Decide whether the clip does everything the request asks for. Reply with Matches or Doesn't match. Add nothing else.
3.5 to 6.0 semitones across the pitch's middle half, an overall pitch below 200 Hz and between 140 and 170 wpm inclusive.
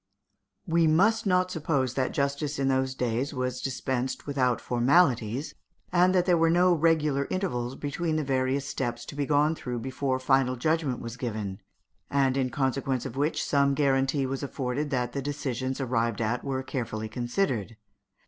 Doesn't match